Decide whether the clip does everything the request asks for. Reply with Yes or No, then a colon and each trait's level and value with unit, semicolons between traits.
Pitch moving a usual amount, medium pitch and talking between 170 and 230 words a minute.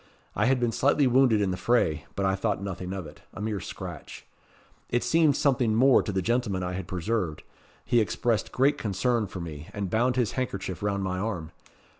No: average, 4.7 semitones; low, 105 Hz; average, 200 wpm